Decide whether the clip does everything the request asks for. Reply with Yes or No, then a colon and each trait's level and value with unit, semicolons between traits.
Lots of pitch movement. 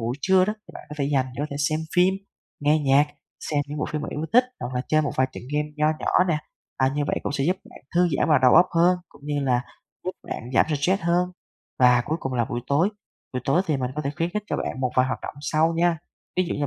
No: average, 4.3 semitones